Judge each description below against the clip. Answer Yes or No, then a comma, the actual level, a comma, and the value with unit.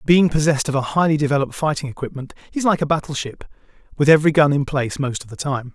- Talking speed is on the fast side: Yes, fast, 230 wpm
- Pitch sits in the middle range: Yes, medium, 145 Hz